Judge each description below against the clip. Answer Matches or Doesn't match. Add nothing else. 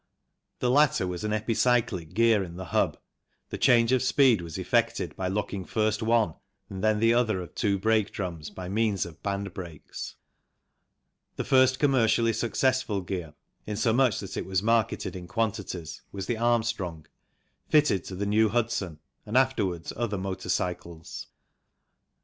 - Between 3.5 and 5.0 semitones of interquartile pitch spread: Matches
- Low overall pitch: Matches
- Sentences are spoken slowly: Doesn't match